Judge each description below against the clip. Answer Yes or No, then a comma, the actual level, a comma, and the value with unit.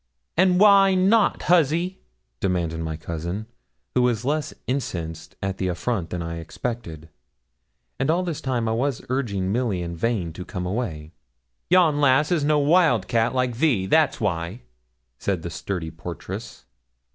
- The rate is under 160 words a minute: Yes, average, 150 wpm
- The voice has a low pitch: Yes, low, 115 Hz